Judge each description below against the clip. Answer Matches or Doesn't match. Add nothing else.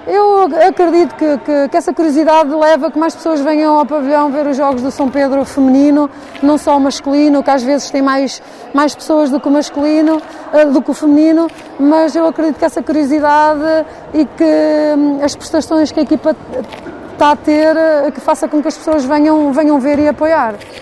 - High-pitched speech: Matches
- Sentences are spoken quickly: Matches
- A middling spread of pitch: Doesn't match